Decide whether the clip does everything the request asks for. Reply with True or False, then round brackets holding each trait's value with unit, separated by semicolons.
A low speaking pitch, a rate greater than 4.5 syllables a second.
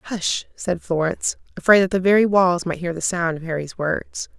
False (180 Hz; 5.0 syllables/s)